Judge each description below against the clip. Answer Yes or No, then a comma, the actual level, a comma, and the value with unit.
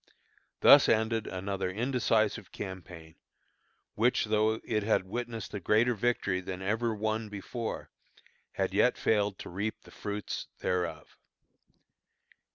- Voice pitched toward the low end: Yes, low, 105 Hz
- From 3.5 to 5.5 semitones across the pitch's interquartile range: No, average, 2.9 semitones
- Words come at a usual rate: No, slow, 120 wpm